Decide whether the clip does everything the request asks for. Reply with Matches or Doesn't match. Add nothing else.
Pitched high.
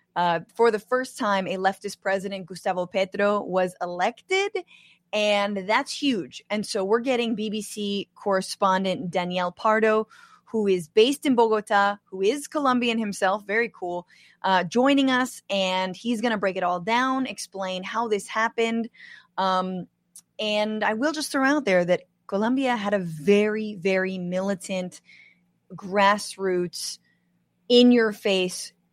Matches